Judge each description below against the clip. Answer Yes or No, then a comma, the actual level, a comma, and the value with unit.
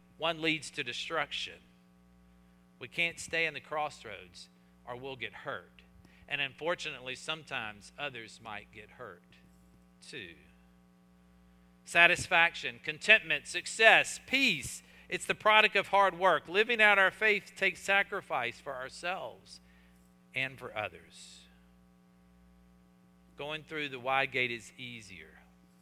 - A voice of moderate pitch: No, low, 125 Hz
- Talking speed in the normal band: No, slow, 115 wpm